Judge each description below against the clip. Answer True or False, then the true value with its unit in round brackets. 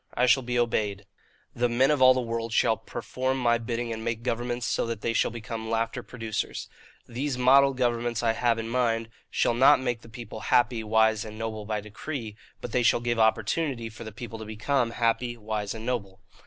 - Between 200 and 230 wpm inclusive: True (205 wpm)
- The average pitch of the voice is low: True (115 Hz)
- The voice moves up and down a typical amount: False (1.8 semitones)